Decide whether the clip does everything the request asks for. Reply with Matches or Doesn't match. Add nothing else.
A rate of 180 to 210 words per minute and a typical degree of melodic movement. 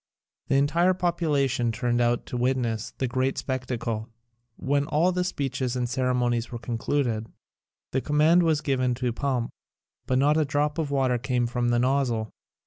Doesn't match